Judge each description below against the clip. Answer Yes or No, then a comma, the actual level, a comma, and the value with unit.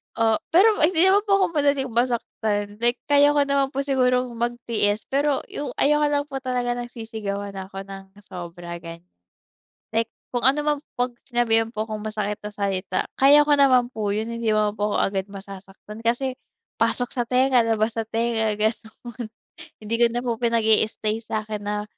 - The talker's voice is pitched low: No, high, 230 Hz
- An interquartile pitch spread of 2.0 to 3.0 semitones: No, average, 3.7 semitones